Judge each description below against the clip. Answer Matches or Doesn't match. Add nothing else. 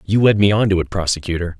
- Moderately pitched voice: Doesn't match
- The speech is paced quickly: Matches